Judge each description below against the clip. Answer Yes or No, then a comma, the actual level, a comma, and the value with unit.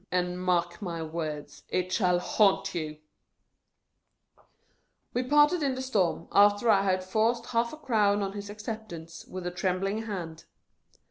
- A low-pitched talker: No, high, 195 Hz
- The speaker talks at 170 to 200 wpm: No, average, 150 wpm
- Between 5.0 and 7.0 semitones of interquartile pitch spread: No, average, 3.7 semitones